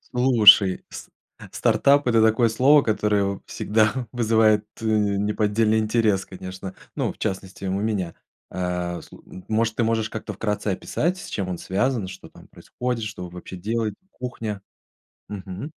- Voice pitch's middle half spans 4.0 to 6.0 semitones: No, average, 3.0 semitones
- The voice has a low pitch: Yes, low, 105 Hz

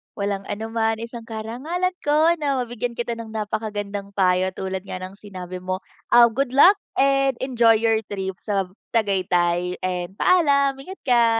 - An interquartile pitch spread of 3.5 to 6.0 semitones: Yes, average, 4.7 semitones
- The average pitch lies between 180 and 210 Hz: No, high, 220 Hz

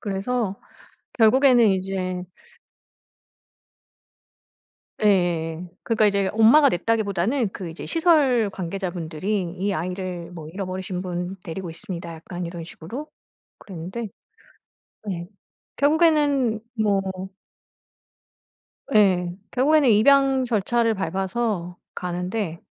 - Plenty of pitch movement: No, average, 4.6 semitones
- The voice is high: Yes, high, 195 Hz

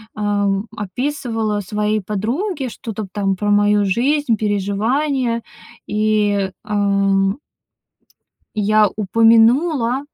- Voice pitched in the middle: No, high, 215 Hz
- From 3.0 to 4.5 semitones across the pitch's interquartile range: No, narrow, 2.5 semitones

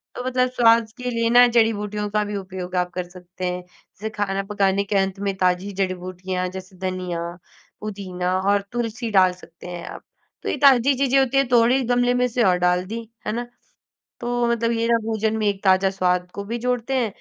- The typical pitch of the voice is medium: No, high, 205 Hz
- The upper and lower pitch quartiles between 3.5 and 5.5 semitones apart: Yes, average, 4.2 semitones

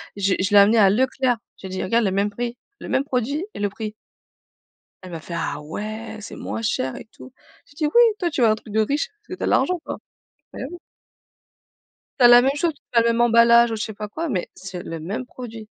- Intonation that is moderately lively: Yes, average, 3.9 semitones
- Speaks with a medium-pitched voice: No, high, 225 Hz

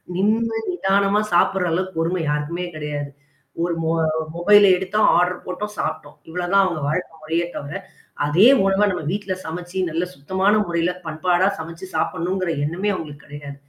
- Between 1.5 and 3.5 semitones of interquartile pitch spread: Yes, average, 3.2 semitones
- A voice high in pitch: No, medium, 175 Hz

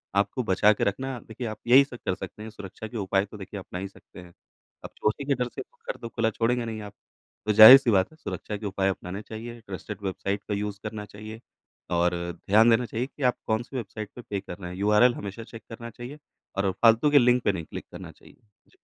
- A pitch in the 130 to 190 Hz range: No, low, 110 Hz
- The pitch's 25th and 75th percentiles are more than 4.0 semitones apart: No, average, 3.2 semitones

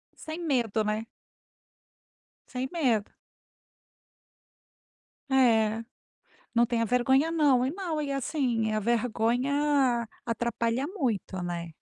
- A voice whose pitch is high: Yes, high, 245 Hz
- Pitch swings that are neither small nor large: Yes, average, 3.8 semitones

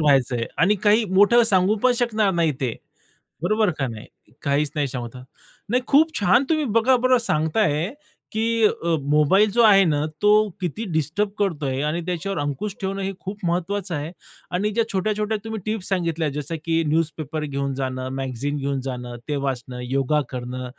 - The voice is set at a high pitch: No, medium, 170 Hz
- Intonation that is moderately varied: No, wide, 6.9 semitones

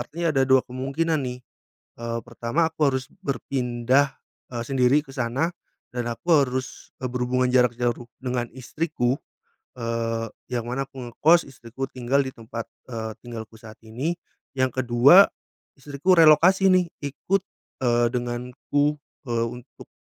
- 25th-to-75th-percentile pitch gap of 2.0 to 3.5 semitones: Yes, average, 2.8 semitones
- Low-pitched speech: Yes, low, 125 Hz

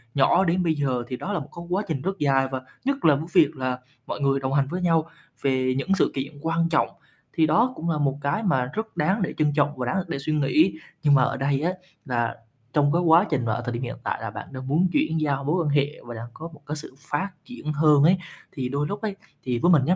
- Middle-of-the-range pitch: Yes, medium, 150 Hz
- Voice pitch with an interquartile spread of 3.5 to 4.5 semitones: Yes, average, 3.9 semitones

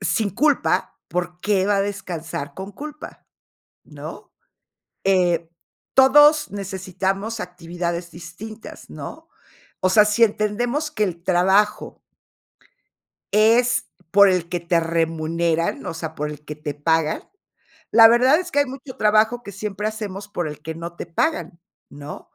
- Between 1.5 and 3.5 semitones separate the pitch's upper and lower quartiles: No, average, 4.5 semitones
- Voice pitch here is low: No, high, 190 Hz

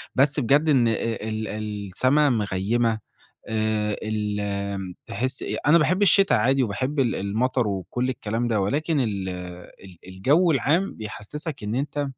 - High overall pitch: No, low, 115 Hz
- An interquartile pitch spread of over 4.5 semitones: Yes, average, 5.1 semitones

